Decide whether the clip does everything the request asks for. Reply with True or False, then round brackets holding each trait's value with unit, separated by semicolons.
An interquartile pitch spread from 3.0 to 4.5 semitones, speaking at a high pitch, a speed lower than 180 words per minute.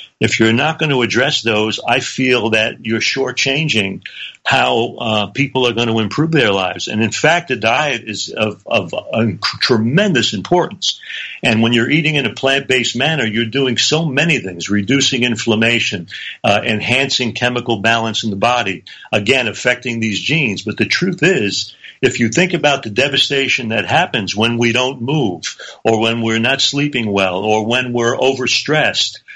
False (3.6 semitones; 120 Hz; 170 wpm)